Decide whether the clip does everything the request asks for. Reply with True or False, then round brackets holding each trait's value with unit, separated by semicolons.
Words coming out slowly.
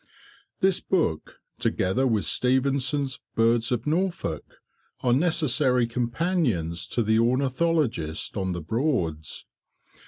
True (100 wpm)